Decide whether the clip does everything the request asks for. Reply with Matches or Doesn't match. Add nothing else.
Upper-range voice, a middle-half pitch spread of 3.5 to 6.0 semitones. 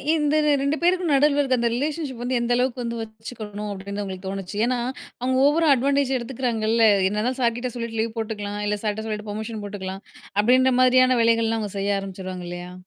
Matches